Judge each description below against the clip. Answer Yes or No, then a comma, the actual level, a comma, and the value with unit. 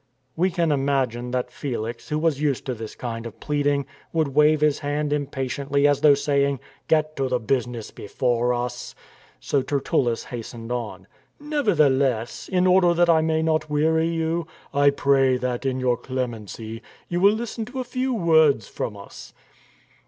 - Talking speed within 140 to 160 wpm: No, average, 170 wpm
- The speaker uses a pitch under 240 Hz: Yes, medium, 140 Hz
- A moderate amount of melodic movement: Yes, average, 4.4 semitones